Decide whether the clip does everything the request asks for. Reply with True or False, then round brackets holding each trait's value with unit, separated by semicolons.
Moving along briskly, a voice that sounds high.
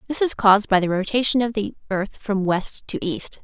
True (225 wpm; 210 Hz)